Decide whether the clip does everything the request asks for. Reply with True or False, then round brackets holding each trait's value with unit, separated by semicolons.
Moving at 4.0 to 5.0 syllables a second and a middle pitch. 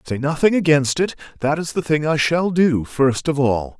True (4.8 syllables/s; 145 Hz)